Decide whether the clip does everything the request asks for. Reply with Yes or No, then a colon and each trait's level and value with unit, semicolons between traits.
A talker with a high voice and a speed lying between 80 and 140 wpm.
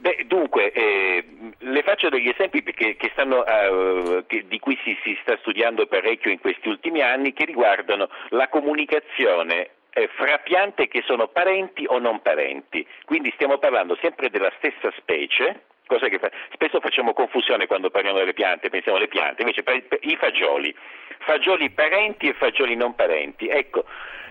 No: very high, 370 Hz; average, 165 wpm